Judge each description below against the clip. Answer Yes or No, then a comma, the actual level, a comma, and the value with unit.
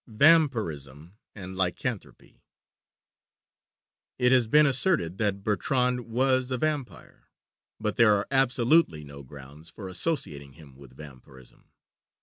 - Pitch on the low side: Yes, low, 105 Hz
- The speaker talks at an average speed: No, slow, 115 wpm